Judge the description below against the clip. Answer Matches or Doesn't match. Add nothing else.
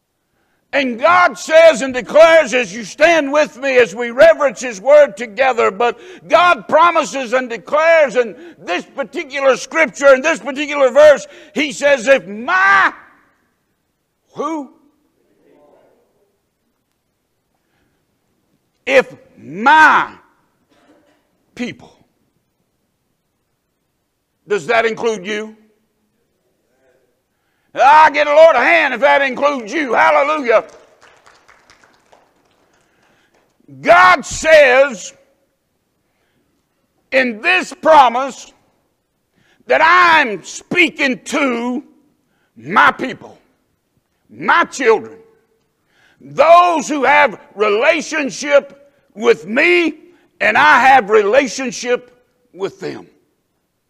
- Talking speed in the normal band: Doesn't match